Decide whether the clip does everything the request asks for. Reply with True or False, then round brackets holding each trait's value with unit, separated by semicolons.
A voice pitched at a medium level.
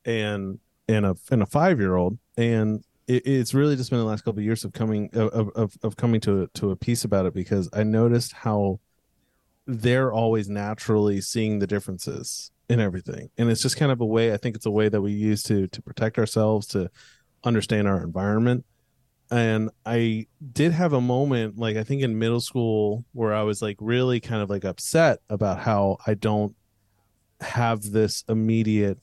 False (110 Hz)